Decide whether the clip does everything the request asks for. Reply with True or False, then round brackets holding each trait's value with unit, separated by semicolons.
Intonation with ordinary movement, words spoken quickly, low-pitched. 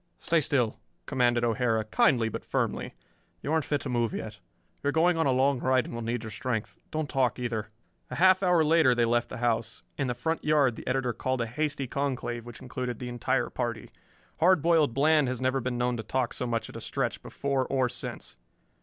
True (3.1 semitones; 215 wpm; 125 Hz)